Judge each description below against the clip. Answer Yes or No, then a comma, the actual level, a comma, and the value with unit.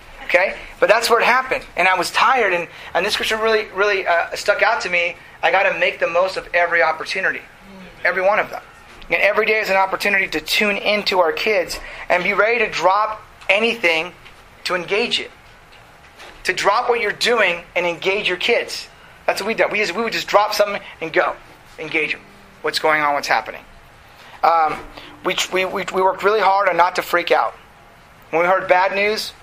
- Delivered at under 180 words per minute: No, average, 200 wpm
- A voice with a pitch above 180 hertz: Yes, high, 190 Hz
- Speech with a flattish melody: No, average, 3.1 semitones